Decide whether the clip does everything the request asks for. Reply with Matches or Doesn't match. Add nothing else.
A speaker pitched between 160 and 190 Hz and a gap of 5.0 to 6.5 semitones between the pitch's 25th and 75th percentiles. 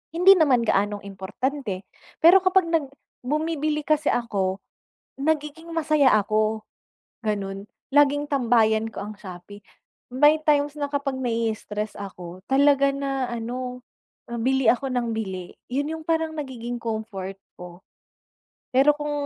Doesn't match